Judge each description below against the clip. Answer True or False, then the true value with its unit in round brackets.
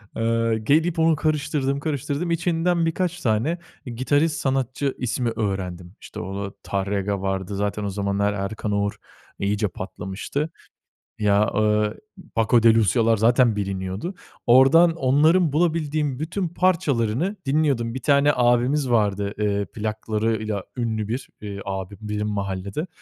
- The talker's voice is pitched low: True (115 Hz)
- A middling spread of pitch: False (6.2 semitones)